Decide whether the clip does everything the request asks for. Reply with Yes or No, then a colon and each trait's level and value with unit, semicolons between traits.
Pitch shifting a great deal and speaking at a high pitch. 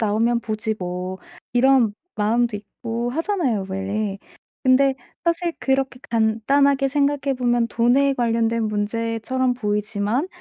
No: average, 3.8 semitones; high, 235 Hz